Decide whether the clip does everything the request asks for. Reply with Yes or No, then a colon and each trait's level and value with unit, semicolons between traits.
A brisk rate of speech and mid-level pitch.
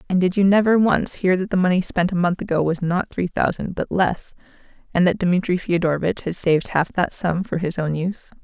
Yes: fast, 230 wpm; medium, 180 Hz